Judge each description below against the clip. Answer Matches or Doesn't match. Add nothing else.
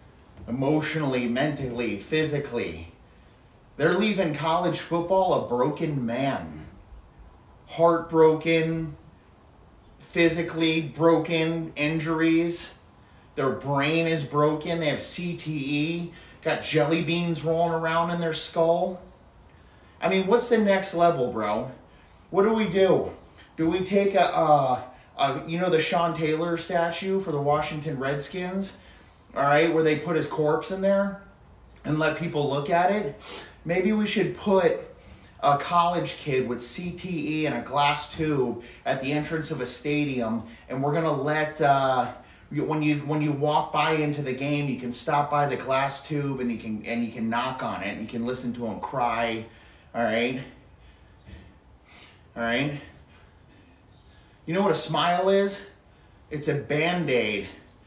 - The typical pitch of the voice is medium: Matches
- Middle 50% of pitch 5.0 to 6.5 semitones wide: Matches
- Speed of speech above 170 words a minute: Doesn't match